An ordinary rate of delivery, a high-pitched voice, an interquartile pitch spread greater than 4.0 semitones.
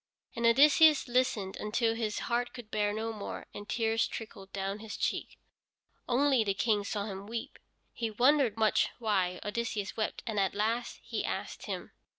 No: average, 165 wpm; high, 220 Hz; narrow, 2.4 semitones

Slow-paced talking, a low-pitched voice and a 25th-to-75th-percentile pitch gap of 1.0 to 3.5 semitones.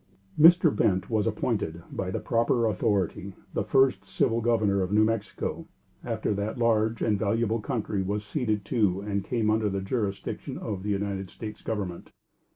No: average, 160 wpm; low, 105 Hz; narrow, 2.5 semitones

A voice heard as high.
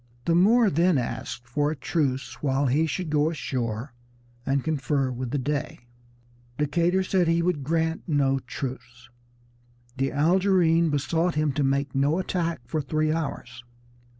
No: medium, 150 Hz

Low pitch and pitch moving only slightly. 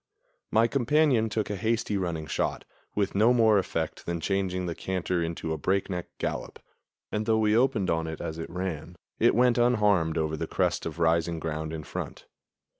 No: very low, 95 Hz; average, 5.1 semitones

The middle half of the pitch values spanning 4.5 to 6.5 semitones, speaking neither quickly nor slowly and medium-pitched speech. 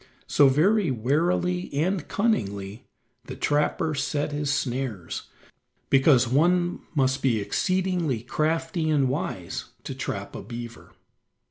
No: average, 4.9 semitones; slow, 115 wpm; medium, 145 Hz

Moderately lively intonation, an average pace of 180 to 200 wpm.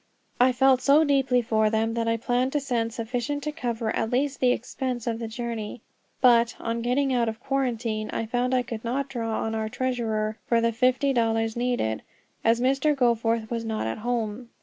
No: narrow, 2.2 semitones; average, 195 wpm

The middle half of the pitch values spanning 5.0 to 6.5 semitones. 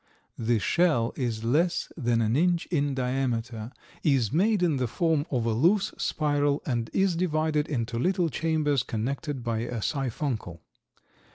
Yes: wide, 5.4 semitones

